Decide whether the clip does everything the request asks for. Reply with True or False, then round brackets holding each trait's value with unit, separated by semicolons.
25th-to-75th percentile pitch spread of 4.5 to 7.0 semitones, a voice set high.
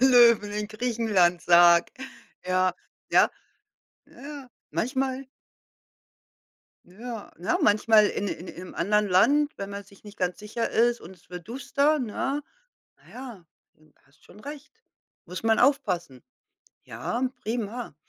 True (5.3 semitones; 215 Hz)